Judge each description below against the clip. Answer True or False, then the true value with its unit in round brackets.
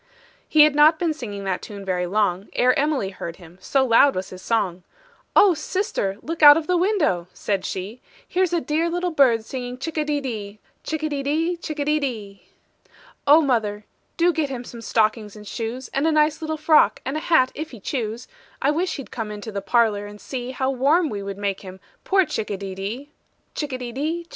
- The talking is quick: True (215 wpm)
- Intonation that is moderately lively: False (6.9 semitones)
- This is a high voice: True (255 Hz)